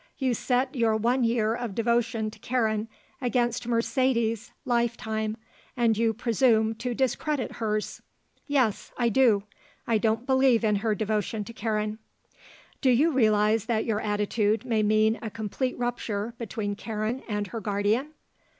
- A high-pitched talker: Yes, high, 225 Hz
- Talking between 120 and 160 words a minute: Yes, average, 150 wpm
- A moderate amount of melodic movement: No, narrow, 2.1 semitones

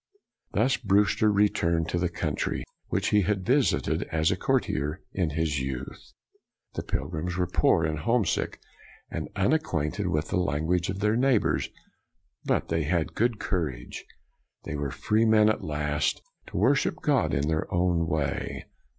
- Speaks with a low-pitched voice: Yes, very low, 85 Hz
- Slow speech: No, average, 155 wpm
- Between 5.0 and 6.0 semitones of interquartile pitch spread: Yes, average, 5.3 semitones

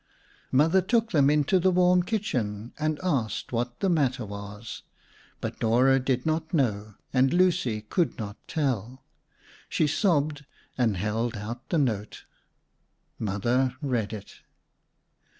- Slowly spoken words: Yes, slow, 130 wpm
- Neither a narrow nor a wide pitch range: No, wide, 6.2 semitones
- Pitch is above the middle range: No, low, 130 Hz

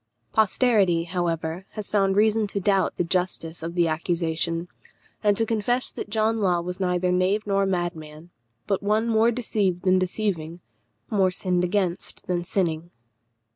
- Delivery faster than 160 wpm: No, average, 150 wpm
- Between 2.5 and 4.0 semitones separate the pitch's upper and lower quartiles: Yes, average, 3.2 semitones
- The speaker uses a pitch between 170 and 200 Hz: Yes, medium, 185 Hz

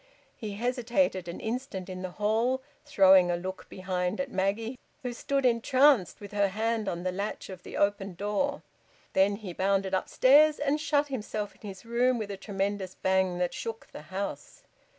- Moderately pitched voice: No, high, 205 Hz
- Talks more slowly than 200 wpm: Yes, average, 175 wpm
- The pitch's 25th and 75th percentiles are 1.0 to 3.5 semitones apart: No, average, 4.5 semitones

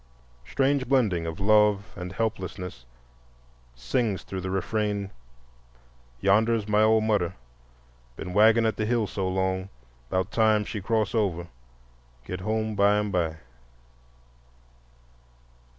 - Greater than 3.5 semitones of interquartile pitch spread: No, average, 2.8 semitones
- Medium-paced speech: No, slow, 115 wpm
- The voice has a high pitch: No, low, 105 Hz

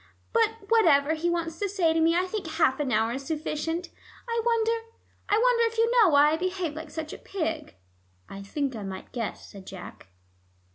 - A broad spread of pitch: Yes, wide, 6.9 semitones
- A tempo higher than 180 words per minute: Yes, average, 200 wpm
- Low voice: No, very high, 330 Hz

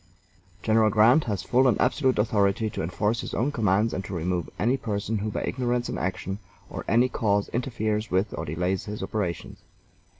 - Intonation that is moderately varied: Yes, average, 3.5 semitones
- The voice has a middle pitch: No, low, 105 Hz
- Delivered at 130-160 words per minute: No, average, 180 wpm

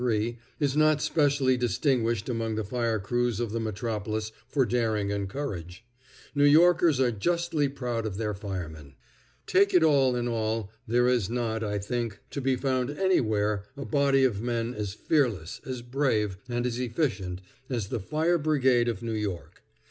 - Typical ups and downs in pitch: Yes, average, 4.2 semitones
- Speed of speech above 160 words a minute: Yes, average, 170 wpm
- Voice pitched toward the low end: Yes, low, 120 Hz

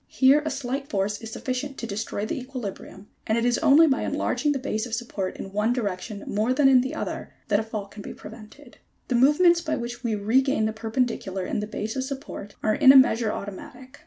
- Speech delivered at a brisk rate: Yes, fast, 220 wpm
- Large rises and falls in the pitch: No, average, 4.0 semitones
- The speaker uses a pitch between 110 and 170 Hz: No, high, 235 Hz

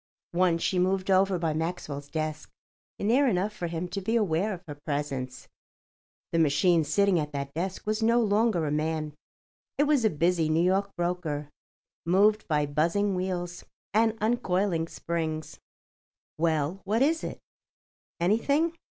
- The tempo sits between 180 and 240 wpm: No, average, 145 wpm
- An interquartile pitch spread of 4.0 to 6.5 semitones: Yes, average, 4.5 semitones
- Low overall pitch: No, medium, 175 Hz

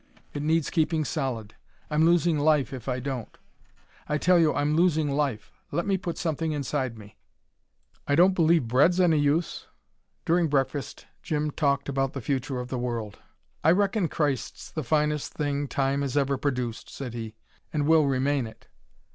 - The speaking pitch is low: No, medium, 145 Hz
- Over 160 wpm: Yes, average, 170 wpm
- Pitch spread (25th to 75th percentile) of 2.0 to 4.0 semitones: Yes, average, 3.3 semitones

